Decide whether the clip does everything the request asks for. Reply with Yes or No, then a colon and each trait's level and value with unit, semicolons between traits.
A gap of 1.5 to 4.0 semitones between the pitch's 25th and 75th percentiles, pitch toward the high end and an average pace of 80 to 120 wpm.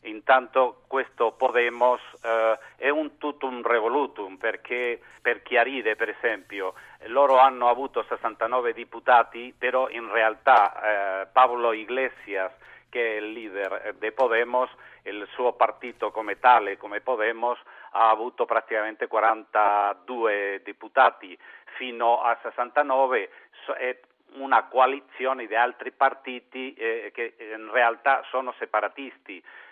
No: average, 2.7 semitones; low, 125 Hz; slow, 115 wpm